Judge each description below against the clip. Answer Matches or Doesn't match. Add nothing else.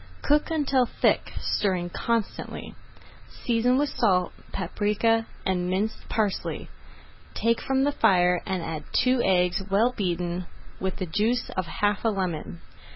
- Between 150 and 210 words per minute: Doesn't match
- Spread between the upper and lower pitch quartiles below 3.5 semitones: Doesn't match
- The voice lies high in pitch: Matches